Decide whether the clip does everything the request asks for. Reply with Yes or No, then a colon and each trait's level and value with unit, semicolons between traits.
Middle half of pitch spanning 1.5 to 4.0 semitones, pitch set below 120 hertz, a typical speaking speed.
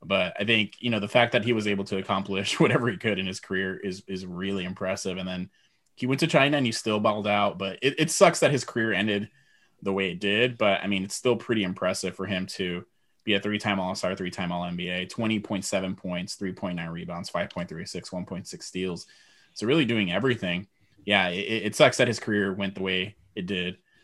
No: average, 2.7 semitones; low, 100 Hz; fast, 215 wpm